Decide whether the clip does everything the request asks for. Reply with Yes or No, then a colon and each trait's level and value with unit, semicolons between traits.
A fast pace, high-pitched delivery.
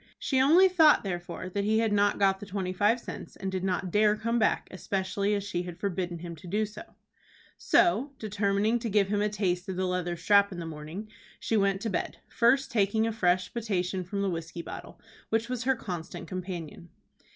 Yes: fast, 210 wpm; high, 200 Hz